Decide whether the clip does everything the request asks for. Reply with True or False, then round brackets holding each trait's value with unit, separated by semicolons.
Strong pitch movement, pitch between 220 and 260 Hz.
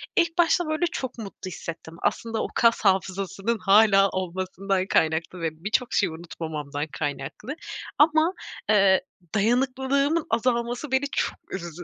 False (6.2 semitones; 200 Hz)